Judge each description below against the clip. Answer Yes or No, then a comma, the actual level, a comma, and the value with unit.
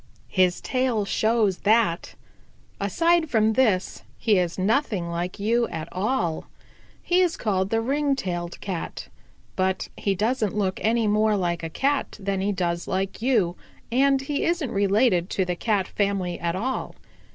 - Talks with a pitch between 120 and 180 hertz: No, high, 205 Hz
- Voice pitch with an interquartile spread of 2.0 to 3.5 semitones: No, average, 4.5 semitones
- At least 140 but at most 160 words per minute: Yes, average, 155 wpm